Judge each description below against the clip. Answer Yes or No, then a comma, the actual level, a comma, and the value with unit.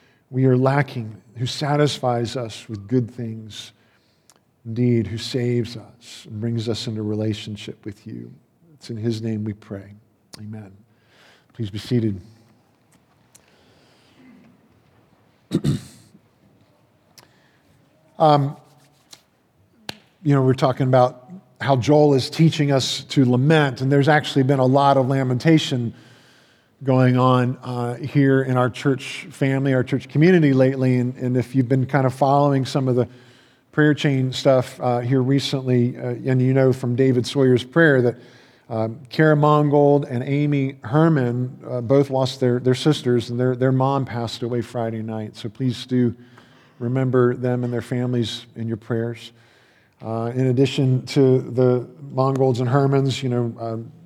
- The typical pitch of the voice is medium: No, low, 125 Hz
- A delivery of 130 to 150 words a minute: Yes, average, 145 wpm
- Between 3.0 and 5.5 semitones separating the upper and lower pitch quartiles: No, narrow, 2.6 semitones